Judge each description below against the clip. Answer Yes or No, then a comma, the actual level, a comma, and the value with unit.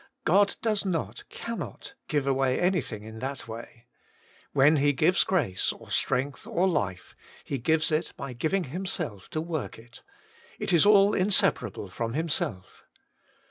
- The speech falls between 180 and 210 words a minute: No, average, 150 wpm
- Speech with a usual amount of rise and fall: No, wide, 6.4 semitones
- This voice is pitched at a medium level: Yes, medium, 150 Hz